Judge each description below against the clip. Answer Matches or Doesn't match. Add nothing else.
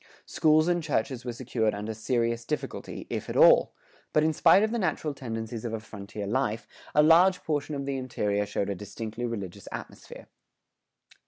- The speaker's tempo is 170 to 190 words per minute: Matches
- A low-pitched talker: Matches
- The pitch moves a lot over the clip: Matches